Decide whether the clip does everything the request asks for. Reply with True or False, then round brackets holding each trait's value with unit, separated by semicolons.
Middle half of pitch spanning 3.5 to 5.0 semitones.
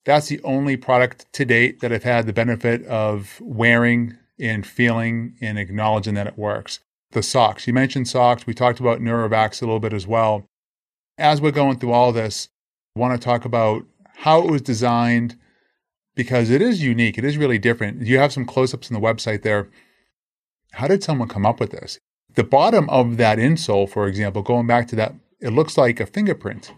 False (2.5 semitones)